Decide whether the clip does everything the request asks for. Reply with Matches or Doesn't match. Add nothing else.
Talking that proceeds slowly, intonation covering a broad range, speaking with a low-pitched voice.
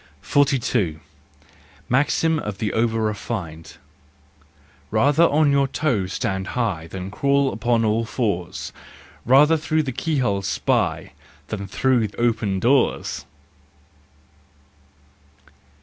Matches